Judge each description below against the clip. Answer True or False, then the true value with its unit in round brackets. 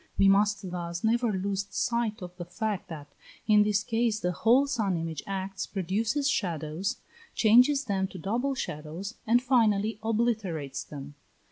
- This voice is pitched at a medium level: False (200 Hz)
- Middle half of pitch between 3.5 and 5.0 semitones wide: True (4.1 semitones)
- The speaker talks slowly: False (150 wpm)